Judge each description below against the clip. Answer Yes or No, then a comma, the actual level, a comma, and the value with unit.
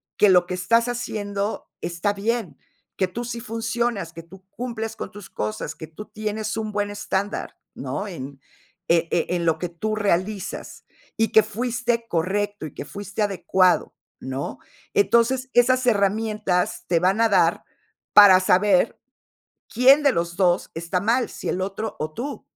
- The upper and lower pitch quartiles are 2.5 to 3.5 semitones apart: No, average, 4.1 semitones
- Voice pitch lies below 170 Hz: No, high, 205 Hz